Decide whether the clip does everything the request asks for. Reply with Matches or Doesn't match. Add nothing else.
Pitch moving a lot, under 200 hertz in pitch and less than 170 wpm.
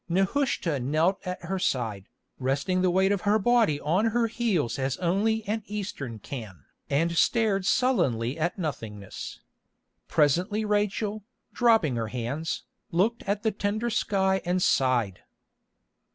Matches